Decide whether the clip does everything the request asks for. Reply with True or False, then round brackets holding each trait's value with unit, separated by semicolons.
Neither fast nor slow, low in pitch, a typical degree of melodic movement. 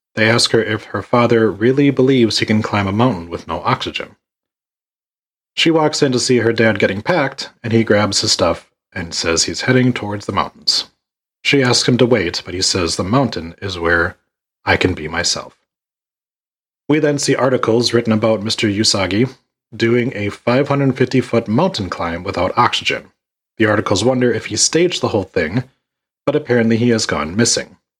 True (180 wpm; 115 Hz; 3.5 semitones)